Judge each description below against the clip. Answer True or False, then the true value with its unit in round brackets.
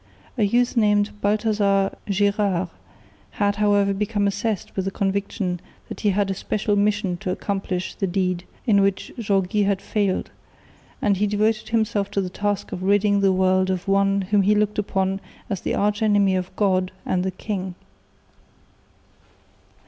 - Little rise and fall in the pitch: True (1.6 semitones)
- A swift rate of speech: False (160 wpm)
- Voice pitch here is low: False (200 Hz)